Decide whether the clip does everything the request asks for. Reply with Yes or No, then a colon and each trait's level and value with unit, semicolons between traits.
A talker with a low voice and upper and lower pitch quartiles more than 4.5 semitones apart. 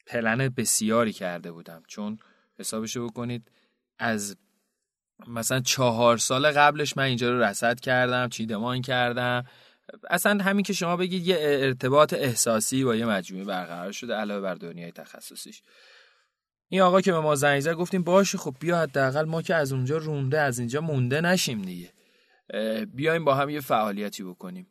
Yes: low, 125 Hz; wide, 5.4 semitones